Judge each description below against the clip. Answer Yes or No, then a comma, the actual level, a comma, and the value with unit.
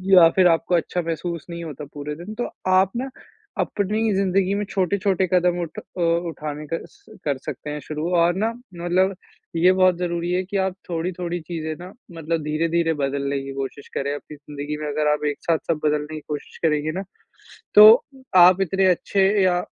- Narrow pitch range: No, average, 3.5 semitones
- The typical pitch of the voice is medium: Yes, medium, 170 Hz